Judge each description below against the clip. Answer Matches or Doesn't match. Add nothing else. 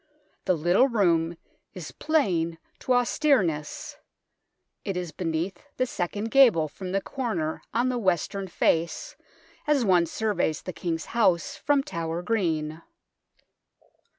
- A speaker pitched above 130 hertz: Matches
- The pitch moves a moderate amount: Doesn't match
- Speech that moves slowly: Matches